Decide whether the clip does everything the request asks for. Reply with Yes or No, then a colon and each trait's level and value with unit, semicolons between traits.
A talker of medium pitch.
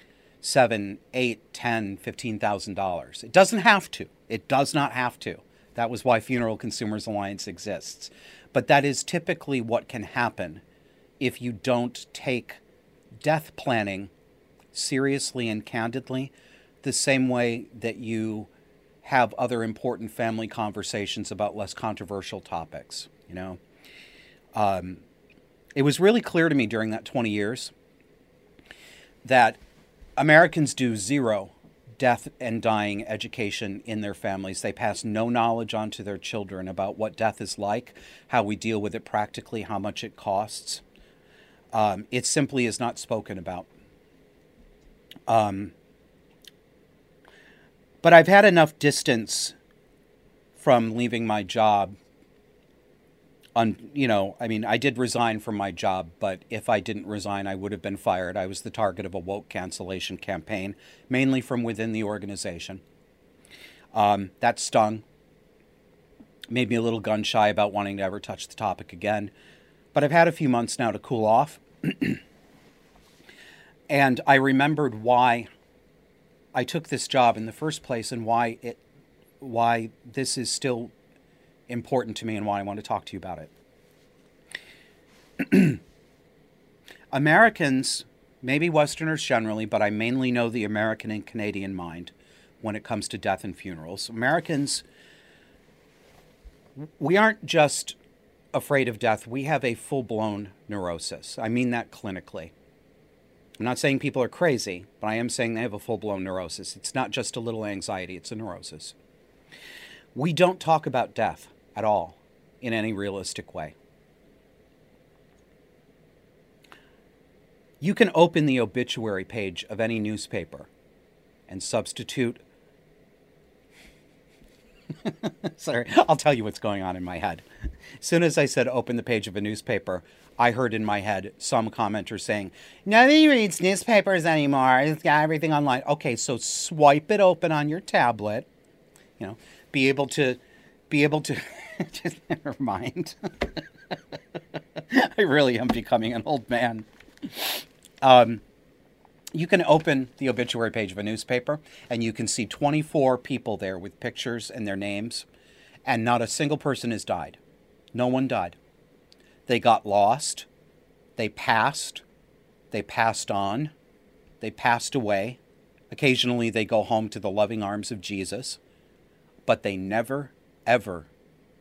No: low, 115 Hz